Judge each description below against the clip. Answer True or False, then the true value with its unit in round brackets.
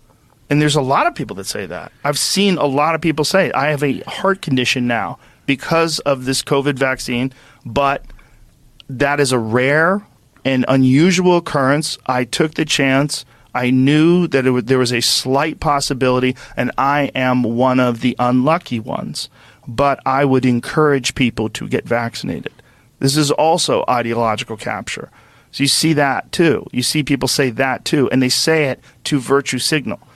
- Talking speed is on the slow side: False (175 wpm)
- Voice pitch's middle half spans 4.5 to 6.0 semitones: False (2.9 semitones)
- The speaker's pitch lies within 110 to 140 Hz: True (135 Hz)